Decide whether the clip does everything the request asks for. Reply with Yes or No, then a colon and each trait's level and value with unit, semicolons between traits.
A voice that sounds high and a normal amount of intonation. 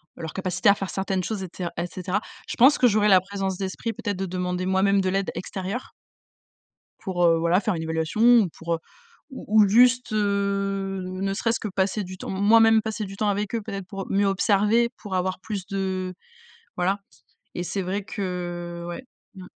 No: high, 195 Hz; narrow, 2.2 semitones